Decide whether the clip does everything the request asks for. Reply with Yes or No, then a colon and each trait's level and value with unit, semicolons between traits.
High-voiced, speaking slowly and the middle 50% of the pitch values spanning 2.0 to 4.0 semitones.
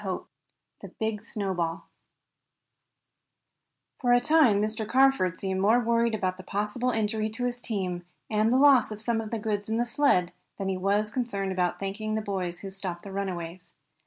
No: high, 210 Hz; average, 190 wpm; average, 3.4 semitones